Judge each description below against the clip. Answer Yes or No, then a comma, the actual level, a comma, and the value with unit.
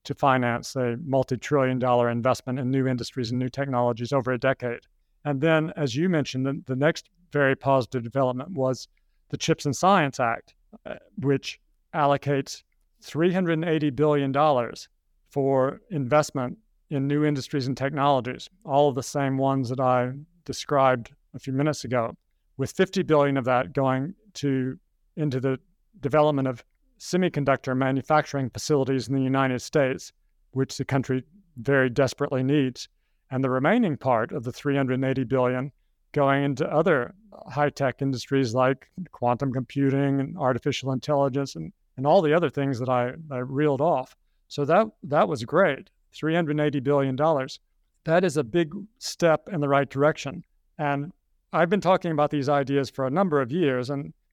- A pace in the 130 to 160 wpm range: Yes, average, 155 wpm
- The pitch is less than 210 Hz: Yes, medium, 140 Hz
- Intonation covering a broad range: No, narrow, 2.5 semitones